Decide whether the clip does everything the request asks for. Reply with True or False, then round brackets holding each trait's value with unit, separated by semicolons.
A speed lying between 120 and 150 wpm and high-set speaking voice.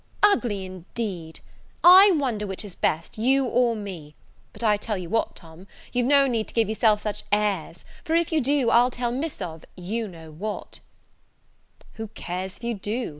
False (185 wpm; 215 Hz)